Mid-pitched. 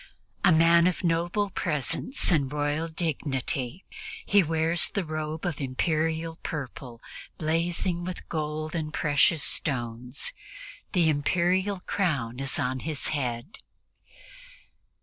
Yes: medium, 160 Hz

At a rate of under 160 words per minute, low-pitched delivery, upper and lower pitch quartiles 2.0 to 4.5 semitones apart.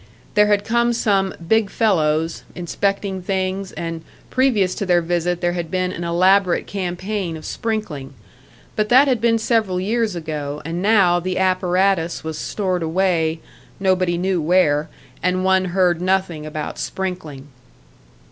No: average, 145 wpm; medium, 185 Hz; average, 2.7 semitones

